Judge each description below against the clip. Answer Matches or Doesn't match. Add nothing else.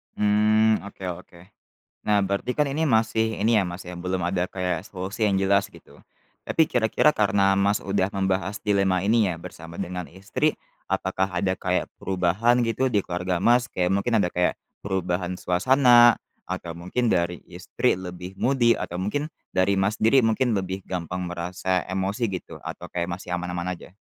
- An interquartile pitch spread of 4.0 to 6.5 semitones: Doesn't match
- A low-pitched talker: Matches